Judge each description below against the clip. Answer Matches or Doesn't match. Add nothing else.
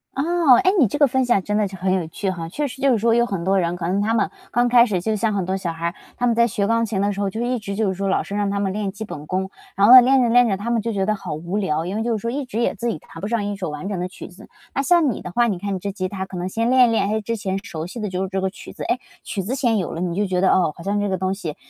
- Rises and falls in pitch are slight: Doesn't match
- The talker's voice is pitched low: Doesn't match